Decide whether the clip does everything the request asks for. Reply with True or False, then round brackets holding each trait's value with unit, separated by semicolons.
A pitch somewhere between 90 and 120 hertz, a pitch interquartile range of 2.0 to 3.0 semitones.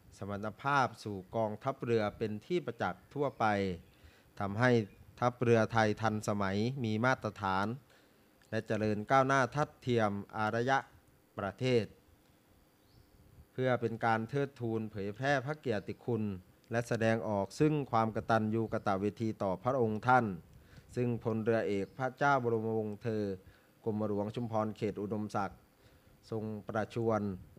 True (110 Hz; 2.6 semitones)